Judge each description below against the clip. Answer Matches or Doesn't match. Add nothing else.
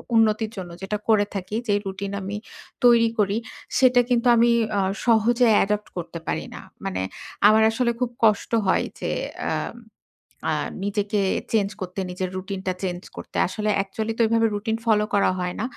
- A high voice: Matches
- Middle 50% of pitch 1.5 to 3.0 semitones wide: Matches